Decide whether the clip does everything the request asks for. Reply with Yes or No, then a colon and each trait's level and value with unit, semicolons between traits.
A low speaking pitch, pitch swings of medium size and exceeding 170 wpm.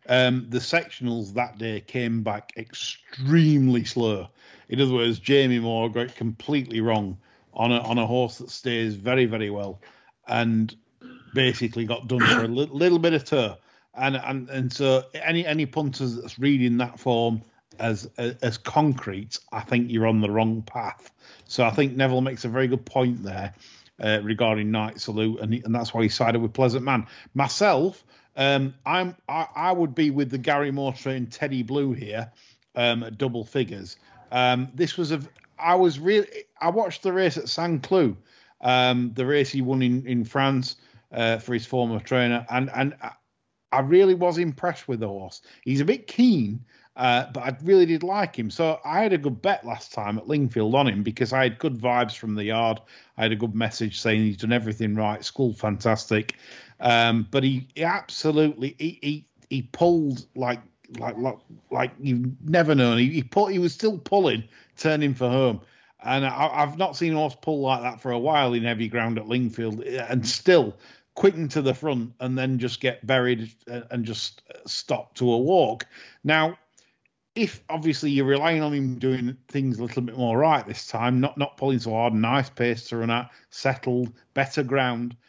Yes: low, 125 Hz; average, 3.4 semitones; average, 190 wpm